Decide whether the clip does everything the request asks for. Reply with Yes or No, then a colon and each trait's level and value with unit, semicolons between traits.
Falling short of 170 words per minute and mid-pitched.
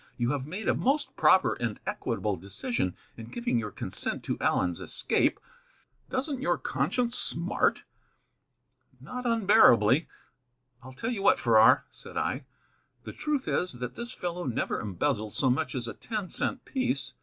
Yes: average, 155 wpm; medium, 145 Hz